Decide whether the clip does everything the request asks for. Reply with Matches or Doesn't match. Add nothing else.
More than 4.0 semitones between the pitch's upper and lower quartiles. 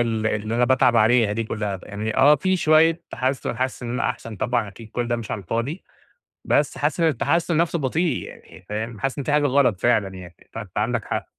Matches